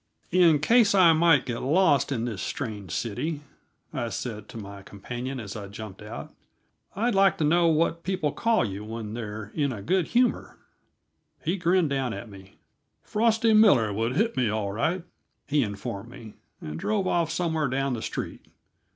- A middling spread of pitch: No, wide, 8.1 semitones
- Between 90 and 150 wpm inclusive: No, average, 175 wpm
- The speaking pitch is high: No, low, 135 Hz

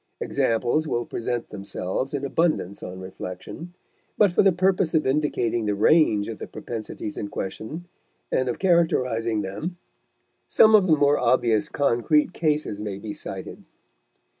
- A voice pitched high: No, low, 125 Hz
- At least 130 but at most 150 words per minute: Yes, average, 145 wpm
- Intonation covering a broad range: Yes, wide, 6.9 semitones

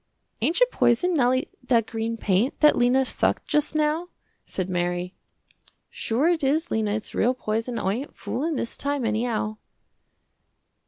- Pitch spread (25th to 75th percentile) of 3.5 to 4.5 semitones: No, wide, 5.4 semitones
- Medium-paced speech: Yes, average, 150 wpm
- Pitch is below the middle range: No, high, 245 Hz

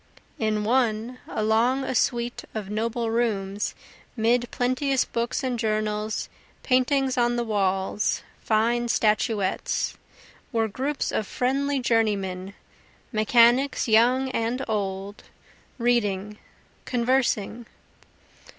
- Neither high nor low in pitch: No, high, 230 Hz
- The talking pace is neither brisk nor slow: No, slow, 95 wpm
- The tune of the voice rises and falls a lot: No, average, 2.7 semitones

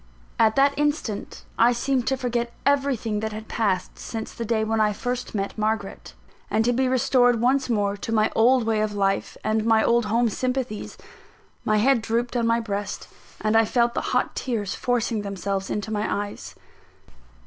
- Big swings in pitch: No, narrow, 2.6 semitones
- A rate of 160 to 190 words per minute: Yes, average, 180 wpm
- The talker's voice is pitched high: Yes, high, 225 Hz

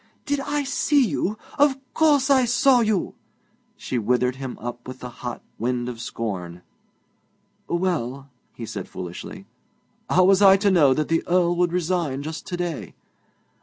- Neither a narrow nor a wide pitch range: No, wide, 8.8 semitones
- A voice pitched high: No, medium, 170 Hz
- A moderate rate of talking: Yes, average, 160 wpm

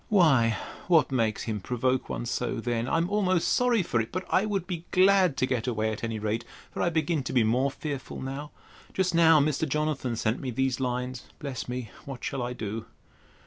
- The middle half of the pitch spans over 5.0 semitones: Yes, wide, 5.6 semitones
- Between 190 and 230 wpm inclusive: Yes, average, 195 wpm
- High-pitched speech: No, low, 130 Hz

